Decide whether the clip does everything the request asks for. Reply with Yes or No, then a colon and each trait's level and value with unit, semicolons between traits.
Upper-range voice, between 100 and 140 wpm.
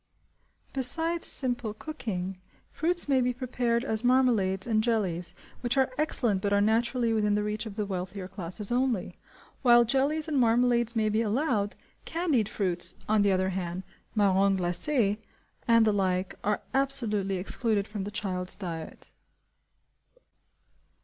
Yes: high, 215 Hz; slow, 135 wpm